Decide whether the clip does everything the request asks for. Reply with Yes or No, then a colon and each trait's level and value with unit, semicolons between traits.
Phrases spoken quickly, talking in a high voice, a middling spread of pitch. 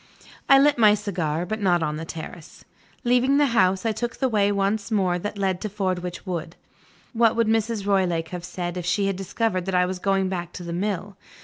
Yes: fast, 215 wpm; high, 195 Hz; average, 3.4 semitones